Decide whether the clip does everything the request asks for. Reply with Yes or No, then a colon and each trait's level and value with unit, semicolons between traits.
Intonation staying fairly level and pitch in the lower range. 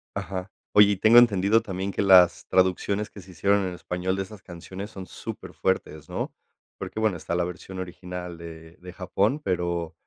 Yes: narrow, 2.2 semitones; very low, 95 Hz